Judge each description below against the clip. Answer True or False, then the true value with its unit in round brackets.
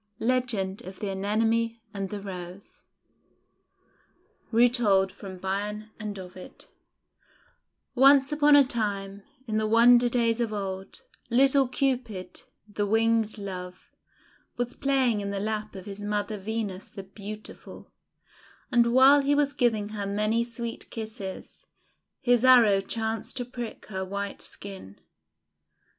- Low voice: False (215 Hz)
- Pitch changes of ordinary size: True (3.4 semitones)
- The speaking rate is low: True (125 wpm)